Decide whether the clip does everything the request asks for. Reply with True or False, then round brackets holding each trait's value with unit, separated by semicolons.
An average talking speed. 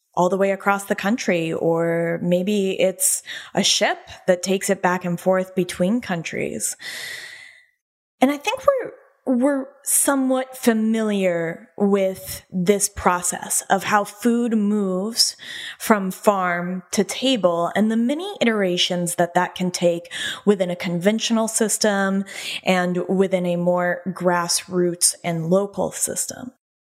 False (125 wpm)